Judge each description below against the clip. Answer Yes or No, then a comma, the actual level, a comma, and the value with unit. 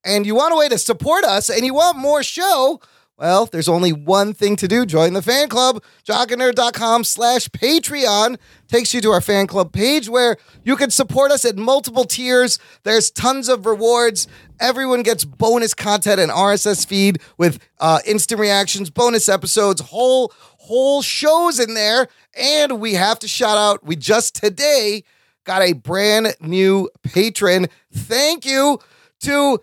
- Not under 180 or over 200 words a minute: No, average, 165 wpm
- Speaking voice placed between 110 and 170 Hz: No, high, 230 Hz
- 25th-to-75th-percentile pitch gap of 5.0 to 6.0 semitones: No, average, 4.5 semitones